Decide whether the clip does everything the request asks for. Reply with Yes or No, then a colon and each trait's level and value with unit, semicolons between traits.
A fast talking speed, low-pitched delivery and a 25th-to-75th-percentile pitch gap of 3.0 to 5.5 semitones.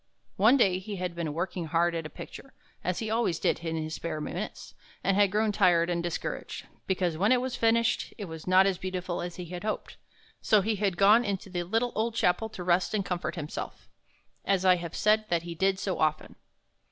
No: fast, 215 wpm; medium, 185 Hz; average, 3.6 semitones